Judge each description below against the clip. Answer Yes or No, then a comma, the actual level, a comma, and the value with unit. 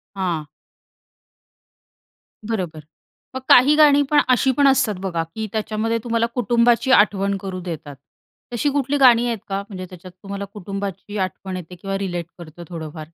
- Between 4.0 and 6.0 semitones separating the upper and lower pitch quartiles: Yes, average, 4.5 semitones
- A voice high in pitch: Yes, high, 200 Hz